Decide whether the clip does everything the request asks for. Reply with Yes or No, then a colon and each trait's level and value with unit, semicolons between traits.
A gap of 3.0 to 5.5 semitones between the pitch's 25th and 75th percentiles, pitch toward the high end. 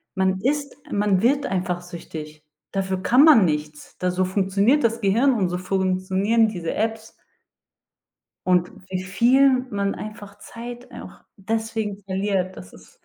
Yes: average, 3.6 semitones; high, 195 Hz